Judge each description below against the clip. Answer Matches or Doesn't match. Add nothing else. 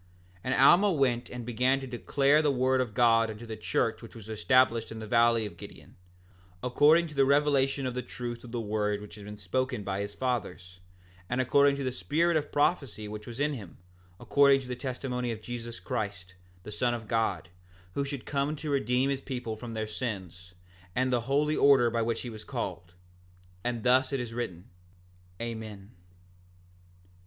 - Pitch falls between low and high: Doesn't match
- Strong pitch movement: Doesn't match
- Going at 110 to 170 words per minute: Doesn't match